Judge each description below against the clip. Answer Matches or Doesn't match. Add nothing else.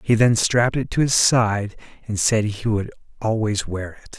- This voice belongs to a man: Matches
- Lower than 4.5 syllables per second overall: Doesn't match